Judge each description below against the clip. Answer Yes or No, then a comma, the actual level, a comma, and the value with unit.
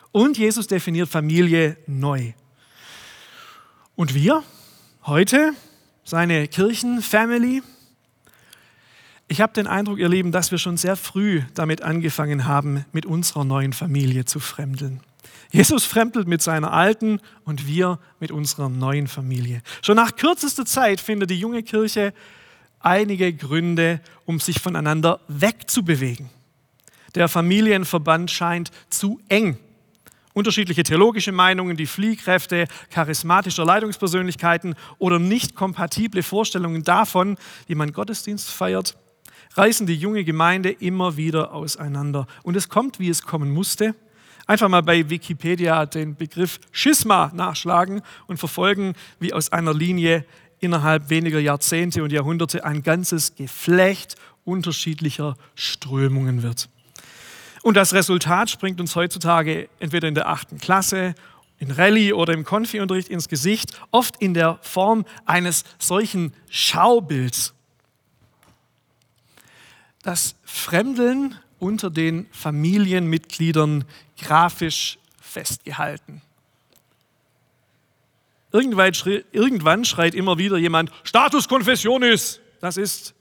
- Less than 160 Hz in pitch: No, medium, 170 Hz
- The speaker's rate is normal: No, slow, 110 wpm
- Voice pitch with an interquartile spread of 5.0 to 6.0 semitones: No, average, 4.4 semitones